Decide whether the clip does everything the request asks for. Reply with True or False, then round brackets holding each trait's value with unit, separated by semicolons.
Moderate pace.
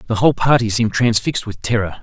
False (210 wpm)